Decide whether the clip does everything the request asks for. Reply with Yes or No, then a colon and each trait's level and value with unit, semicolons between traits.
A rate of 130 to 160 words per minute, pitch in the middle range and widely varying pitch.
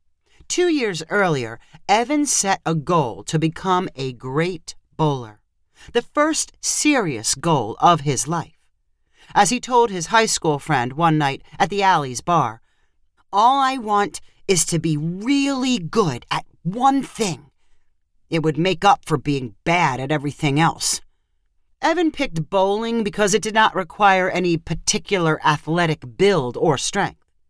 Yes: average, 145 wpm; medium, 170 Hz; wide, 6.1 semitones